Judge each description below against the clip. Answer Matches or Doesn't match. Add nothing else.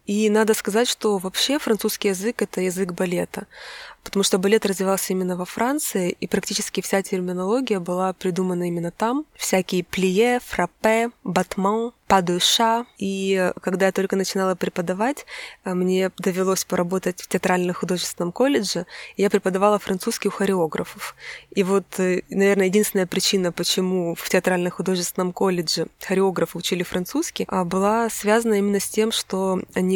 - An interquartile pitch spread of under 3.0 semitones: Matches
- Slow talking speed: Doesn't match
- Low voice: Doesn't match